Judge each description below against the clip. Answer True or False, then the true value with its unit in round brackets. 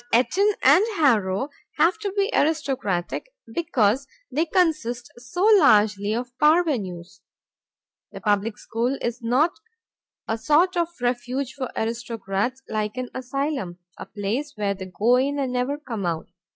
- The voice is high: True (245 Hz)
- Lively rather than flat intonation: True (5.7 semitones)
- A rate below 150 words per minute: True (140 wpm)